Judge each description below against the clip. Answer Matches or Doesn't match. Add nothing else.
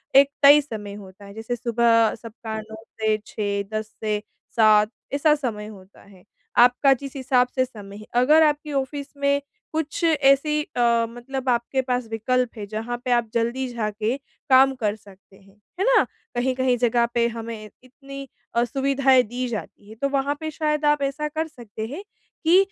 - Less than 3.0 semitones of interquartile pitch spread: Doesn't match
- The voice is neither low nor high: Doesn't match